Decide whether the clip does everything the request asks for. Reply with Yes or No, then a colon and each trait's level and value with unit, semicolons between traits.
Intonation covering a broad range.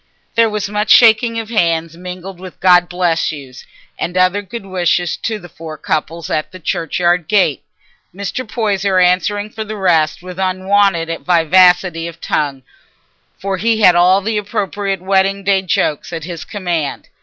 No: average, 3.1 semitones